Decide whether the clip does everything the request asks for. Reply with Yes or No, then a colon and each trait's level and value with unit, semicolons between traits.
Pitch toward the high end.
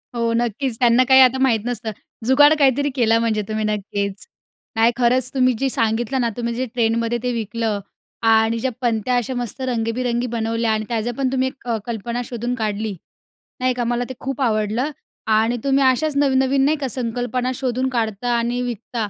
Yes: high, 240 Hz